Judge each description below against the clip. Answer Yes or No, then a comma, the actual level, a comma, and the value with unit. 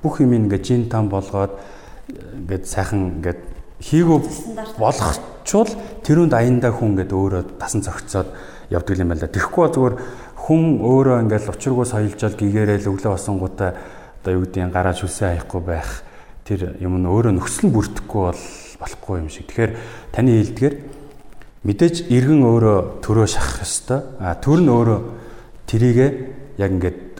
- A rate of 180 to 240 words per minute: No, average, 150 wpm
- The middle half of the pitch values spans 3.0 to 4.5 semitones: No, average, 5.1 semitones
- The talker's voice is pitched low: Yes, low, 105 Hz